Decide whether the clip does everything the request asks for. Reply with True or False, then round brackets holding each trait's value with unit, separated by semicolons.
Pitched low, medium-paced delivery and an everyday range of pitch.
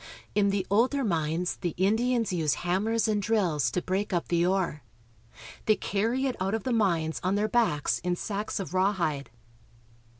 False (195 Hz; 165 wpm; 3.9 semitones)